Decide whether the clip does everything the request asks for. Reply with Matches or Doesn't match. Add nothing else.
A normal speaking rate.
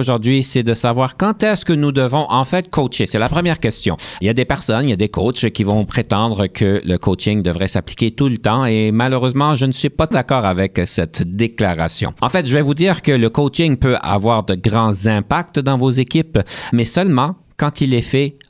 Doesn't match